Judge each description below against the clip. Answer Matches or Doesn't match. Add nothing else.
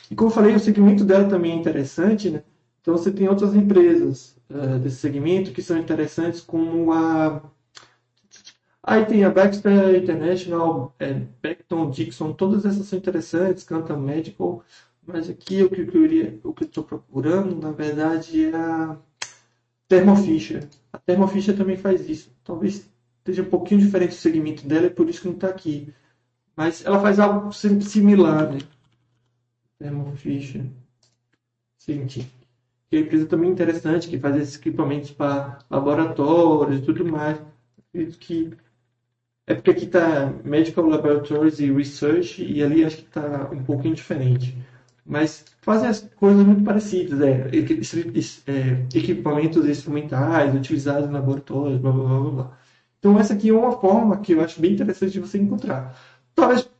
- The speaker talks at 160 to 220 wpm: Doesn't match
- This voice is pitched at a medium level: Matches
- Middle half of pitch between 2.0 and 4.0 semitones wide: Doesn't match